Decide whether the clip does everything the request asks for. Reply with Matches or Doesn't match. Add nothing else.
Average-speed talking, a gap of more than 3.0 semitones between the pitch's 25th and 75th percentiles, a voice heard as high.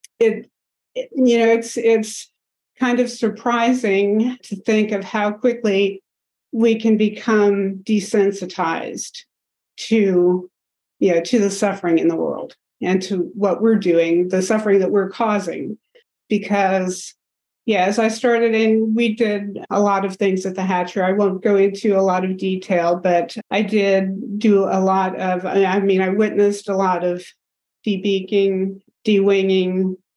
Doesn't match